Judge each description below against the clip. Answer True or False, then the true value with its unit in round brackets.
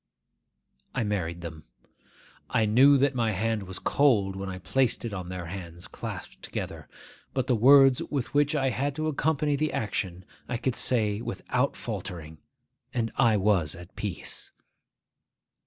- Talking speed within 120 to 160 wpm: True (155 wpm)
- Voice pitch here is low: True (110 Hz)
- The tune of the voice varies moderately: False (6.3 semitones)